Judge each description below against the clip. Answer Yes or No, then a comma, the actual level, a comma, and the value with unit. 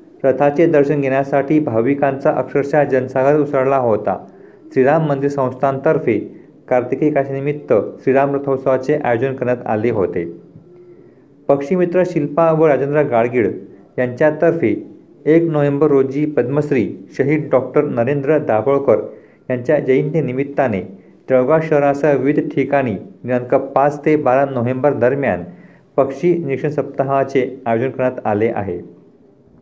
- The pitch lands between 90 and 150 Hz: Yes, medium, 140 Hz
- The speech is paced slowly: No, average, 105 wpm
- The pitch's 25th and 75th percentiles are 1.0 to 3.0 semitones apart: Yes, narrow, 2.4 semitones